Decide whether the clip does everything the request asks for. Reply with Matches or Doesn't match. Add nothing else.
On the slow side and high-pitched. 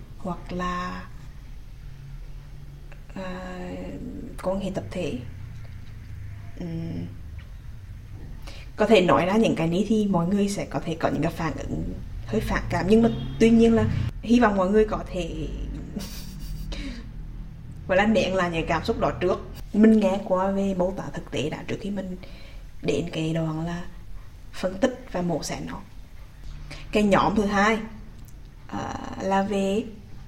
Doesn't match